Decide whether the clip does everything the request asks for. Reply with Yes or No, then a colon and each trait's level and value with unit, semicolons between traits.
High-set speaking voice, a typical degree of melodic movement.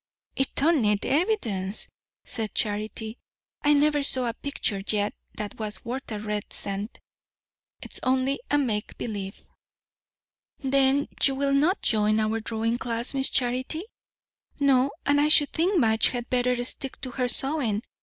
Yes: very high, 250 Hz; average, 4.3 semitones